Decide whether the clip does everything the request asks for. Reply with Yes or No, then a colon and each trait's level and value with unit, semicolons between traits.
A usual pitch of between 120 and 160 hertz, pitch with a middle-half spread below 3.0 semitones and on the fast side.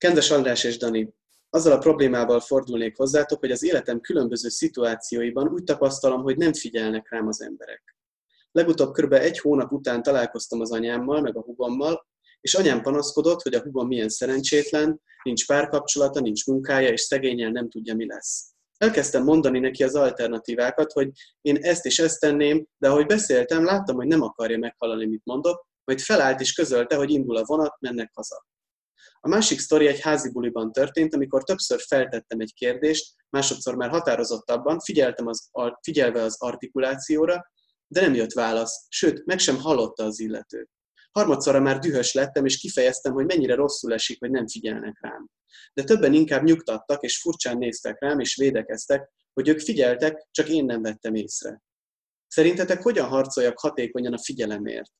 No: low, 135 Hz; average, 4.3 semitones; fast, 165 wpm